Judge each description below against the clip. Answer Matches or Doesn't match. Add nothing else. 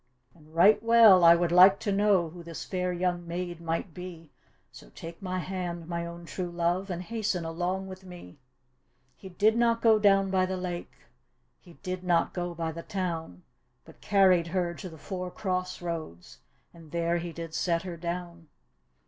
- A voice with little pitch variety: Matches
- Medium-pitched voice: Matches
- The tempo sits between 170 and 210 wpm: Matches